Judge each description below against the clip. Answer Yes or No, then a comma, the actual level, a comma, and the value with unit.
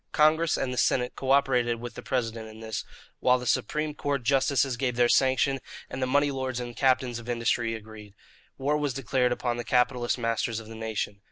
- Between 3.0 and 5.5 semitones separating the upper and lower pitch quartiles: No, narrow, 2.5 semitones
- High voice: No, low, 125 Hz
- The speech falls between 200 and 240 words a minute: Yes, fast, 205 wpm